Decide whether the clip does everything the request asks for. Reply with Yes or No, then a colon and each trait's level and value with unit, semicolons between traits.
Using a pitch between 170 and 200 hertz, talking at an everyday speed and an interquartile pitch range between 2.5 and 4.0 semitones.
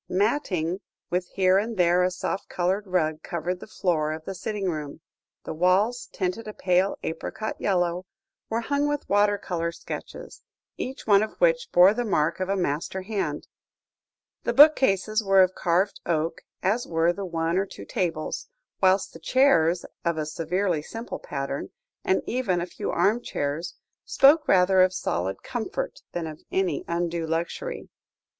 Yes: medium, 185 Hz; average, 160 wpm; average, 3.5 semitones